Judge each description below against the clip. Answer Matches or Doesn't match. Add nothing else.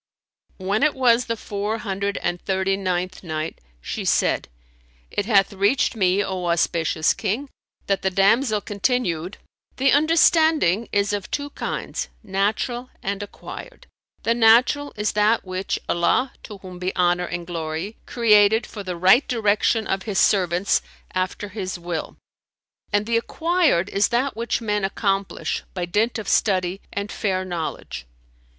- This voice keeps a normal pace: Matches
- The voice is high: Matches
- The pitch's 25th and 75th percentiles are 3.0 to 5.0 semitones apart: Matches